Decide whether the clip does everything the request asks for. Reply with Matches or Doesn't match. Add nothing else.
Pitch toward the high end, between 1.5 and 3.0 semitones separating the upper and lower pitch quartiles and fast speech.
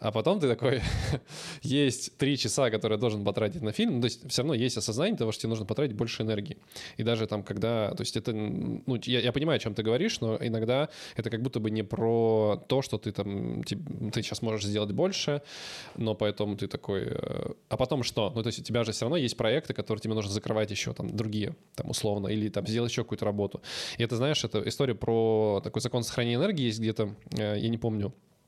Doesn't match